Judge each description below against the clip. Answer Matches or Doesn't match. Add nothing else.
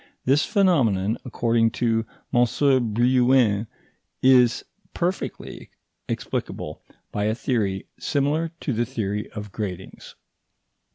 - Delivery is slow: Matches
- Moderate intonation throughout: Matches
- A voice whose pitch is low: Matches